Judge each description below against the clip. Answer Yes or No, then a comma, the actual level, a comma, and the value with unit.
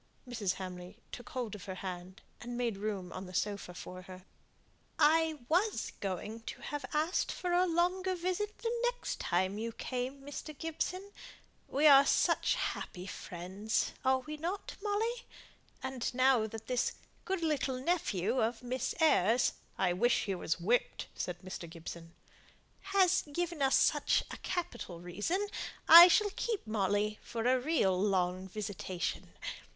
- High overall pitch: Yes, high, 245 Hz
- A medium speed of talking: Yes, average, 155 wpm